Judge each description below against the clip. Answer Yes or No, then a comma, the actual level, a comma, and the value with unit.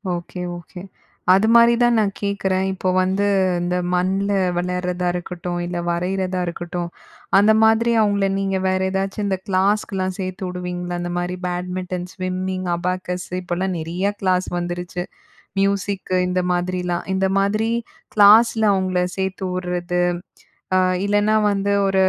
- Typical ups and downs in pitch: No, narrow, 1.7 semitones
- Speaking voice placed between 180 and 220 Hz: Yes, medium, 185 Hz